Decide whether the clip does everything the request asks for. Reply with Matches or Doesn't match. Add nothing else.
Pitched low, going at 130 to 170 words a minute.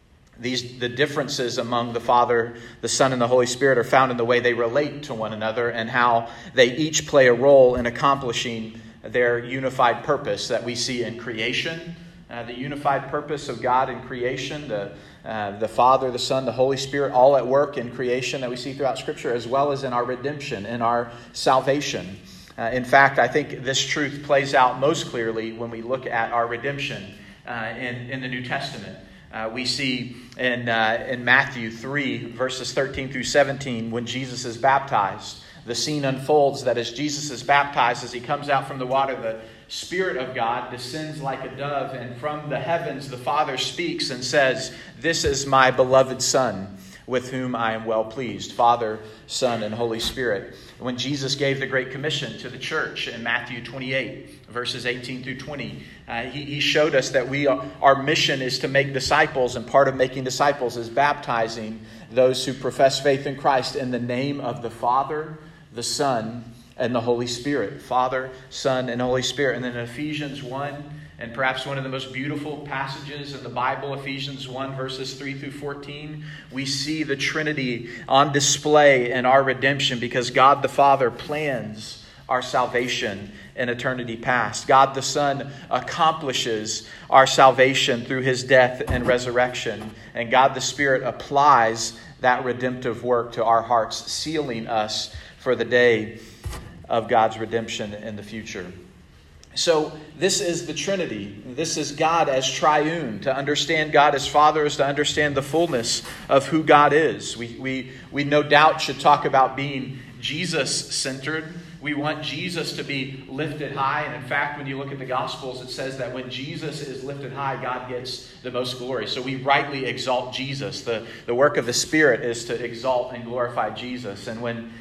Doesn't match